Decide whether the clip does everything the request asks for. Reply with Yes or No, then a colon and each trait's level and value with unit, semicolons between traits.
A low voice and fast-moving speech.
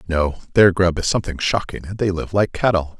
Yes: very low, 90 Hz; fast, 220 wpm